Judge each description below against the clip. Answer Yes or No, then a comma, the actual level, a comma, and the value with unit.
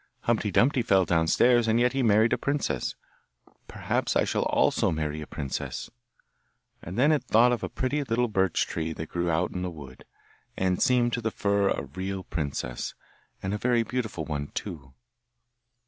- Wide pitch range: Yes, wide, 6.9 semitones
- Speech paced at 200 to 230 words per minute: No, average, 180 wpm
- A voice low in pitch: Yes, very low, 95 Hz